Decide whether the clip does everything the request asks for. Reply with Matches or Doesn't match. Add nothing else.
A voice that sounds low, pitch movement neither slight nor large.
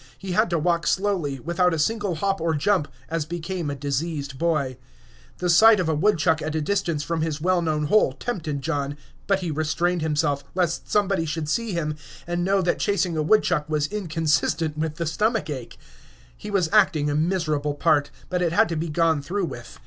Doesn't match